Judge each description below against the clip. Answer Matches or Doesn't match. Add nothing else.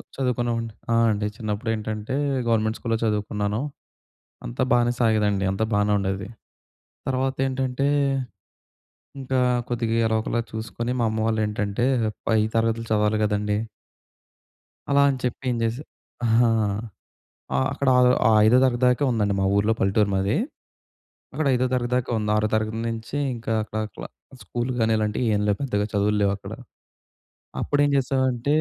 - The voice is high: Doesn't match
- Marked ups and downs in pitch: Doesn't match